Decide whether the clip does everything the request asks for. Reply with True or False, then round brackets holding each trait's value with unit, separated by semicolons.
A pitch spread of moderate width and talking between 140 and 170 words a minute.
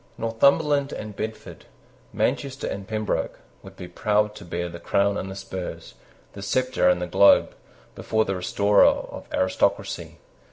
True (3.1 semitones; 150 wpm)